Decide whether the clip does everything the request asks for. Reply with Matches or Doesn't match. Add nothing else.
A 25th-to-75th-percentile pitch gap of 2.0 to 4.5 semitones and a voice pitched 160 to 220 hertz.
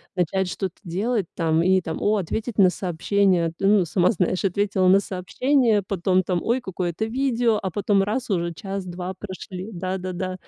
Matches